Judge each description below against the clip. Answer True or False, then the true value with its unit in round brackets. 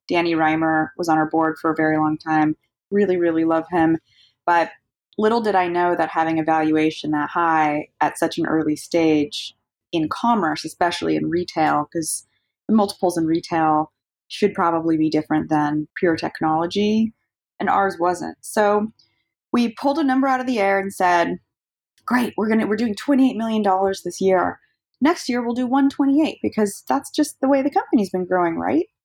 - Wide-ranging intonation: True (5.8 semitones)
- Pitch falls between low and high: True (175 Hz)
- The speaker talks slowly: False (180 wpm)